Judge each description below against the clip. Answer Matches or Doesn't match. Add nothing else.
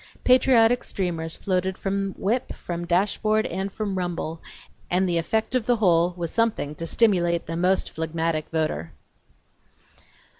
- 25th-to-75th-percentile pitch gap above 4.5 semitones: Doesn't match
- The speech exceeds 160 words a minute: Doesn't match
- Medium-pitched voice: Matches